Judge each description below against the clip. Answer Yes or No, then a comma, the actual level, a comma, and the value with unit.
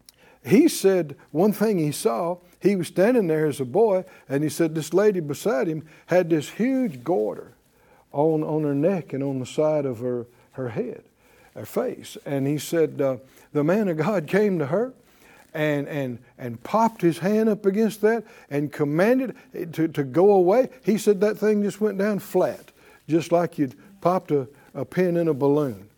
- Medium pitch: Yes, medium, 165 Hz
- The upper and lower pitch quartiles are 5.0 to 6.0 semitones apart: Yes, wide, 5.5 semitones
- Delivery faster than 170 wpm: Yes, average, 190 wpm